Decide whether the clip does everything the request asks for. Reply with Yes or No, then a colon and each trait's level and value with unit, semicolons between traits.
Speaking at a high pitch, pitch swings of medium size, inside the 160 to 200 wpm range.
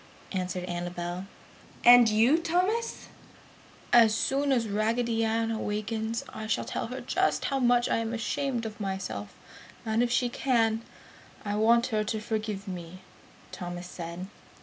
No: high, 220 Hz; average, 3.8 semitones; average, 145 wpm